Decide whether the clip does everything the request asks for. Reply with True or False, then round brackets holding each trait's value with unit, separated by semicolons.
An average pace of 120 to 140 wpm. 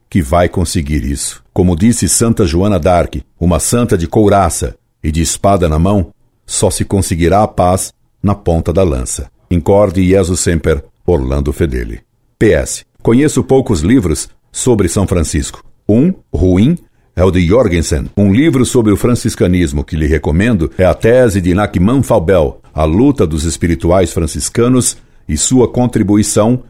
False (150 wpm)